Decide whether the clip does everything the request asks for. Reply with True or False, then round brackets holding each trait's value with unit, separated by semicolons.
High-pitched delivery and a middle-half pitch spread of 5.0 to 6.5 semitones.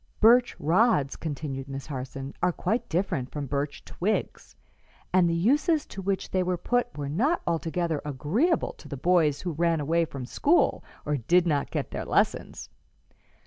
False (170 Hz; 5.3 semitones)